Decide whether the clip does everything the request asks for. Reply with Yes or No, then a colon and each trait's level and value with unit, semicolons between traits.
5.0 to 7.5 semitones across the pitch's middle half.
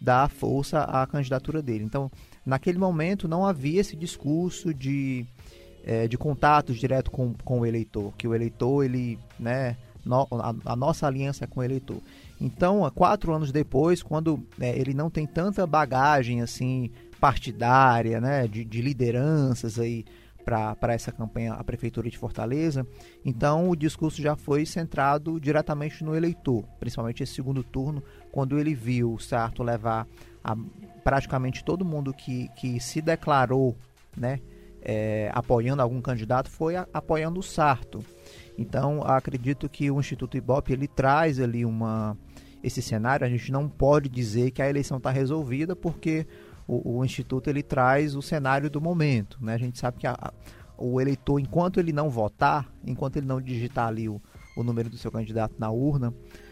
No: average, 4.0 semitones